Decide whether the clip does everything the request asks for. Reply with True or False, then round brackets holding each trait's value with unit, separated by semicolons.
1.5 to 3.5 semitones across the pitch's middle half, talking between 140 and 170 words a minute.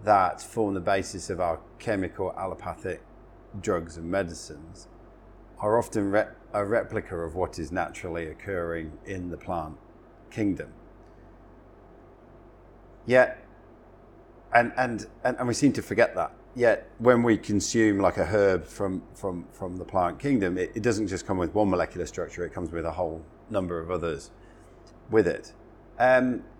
False (4.9 semitones; 155 wpm)